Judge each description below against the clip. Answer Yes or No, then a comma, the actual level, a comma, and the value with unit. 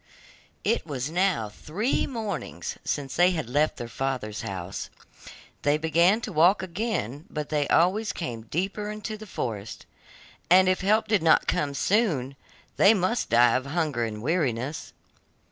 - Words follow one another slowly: No, average, 150 wpm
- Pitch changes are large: Yes, wide, 7.1 semitones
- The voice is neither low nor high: Yes, medium, 155 Hz